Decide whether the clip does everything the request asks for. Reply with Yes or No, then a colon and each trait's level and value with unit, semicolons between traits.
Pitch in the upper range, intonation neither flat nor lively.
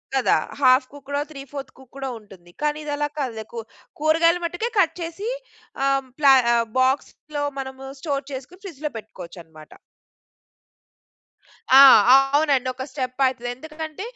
Yes: very high, 275 Hz; average, 3.1 semitones